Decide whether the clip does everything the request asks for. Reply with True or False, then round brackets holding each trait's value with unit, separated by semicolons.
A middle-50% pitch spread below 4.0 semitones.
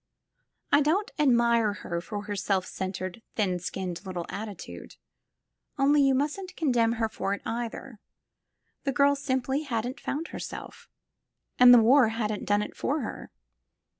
False (5.2 semitones)